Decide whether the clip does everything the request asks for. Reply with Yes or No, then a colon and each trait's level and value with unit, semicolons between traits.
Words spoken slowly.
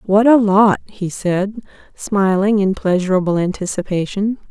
Yes: slow, 120 wpm